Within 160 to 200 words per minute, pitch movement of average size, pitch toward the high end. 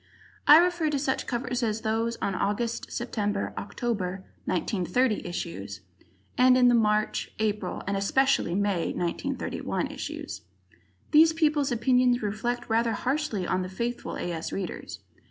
No: slow, 135 wpm; average, 4.3 semitones; high, 230 Hz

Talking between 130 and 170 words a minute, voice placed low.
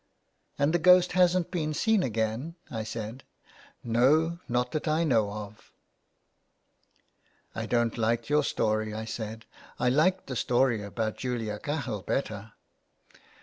Yes: average, 155 wpm; low, 120 Hz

